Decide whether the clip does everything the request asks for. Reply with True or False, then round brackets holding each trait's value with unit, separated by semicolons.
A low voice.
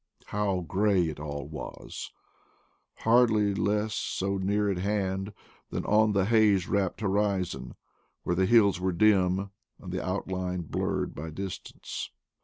True (95 Hz)